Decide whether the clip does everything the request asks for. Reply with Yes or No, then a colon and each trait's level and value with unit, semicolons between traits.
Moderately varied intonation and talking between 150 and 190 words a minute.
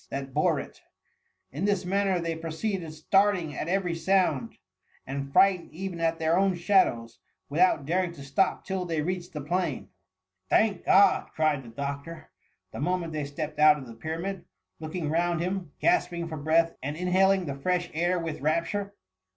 Yes: average, 3.5 semitones; average, 175 wpm